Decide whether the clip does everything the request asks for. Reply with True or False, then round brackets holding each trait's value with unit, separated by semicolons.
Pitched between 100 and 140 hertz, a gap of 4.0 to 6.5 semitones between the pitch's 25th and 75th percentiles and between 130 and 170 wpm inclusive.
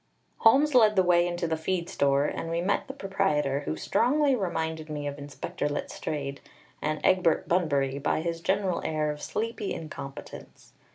False (165 Hz; 4.6 semitones; 165 wpm)